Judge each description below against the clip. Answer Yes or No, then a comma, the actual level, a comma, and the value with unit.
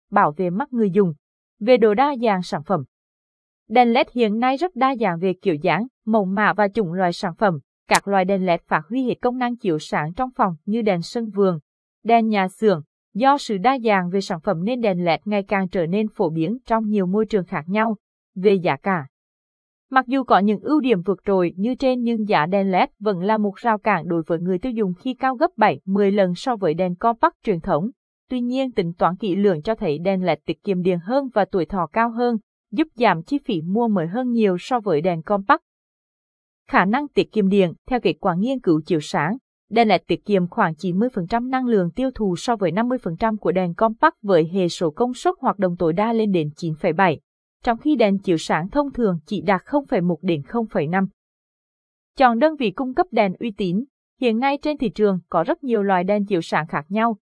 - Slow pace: No, average, 225 wpm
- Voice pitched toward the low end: No, high, 210 Hz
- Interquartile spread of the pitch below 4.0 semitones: No, average, 4.3 semitones